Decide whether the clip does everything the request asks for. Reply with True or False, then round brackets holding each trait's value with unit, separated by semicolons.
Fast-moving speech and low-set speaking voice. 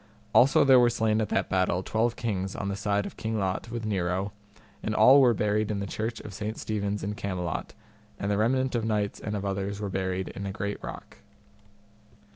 True (210 wpm; 105 Hz)